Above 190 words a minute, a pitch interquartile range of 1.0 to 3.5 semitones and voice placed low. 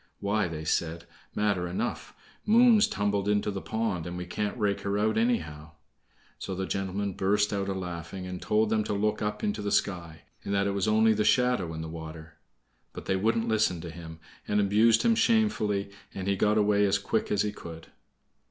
Yes: average, 200 wpm; average, 3.1 semitones; low, 100 Hz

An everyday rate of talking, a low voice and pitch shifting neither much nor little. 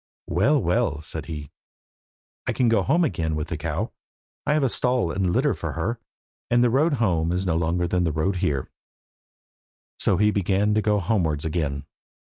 No: average, 180 wpm; very low, 95 Hz; wide, 6.0 semitones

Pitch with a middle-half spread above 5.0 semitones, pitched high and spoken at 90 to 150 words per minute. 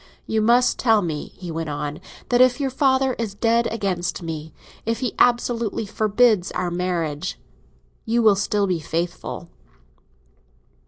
Yes: wide, 5.4 semitones; high, 205 Hz; average, 145 wpm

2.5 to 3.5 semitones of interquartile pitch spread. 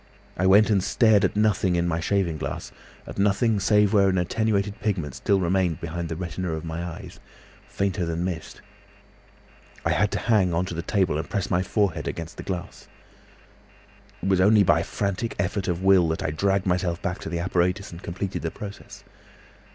Yes: average, 2.8 semitones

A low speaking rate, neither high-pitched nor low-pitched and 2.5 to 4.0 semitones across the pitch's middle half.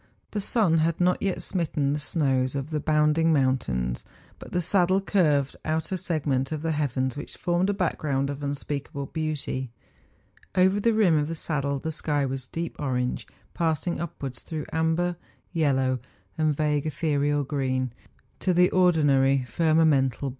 No: average, 170 wpm; medium, 150 Hz; average, 3.4 semitones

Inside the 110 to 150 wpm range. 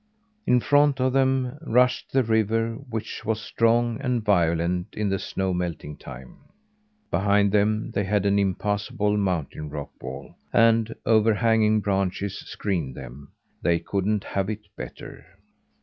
Yes: slow, 135 wpm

